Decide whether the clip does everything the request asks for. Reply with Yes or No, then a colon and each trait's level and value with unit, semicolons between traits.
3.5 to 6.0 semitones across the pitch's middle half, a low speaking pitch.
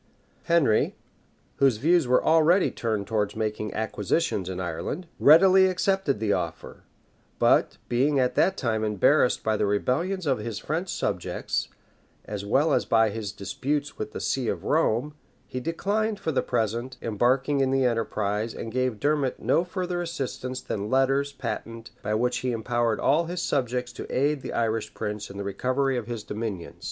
Yes: average, 5.3 semitones; low, 125 Hz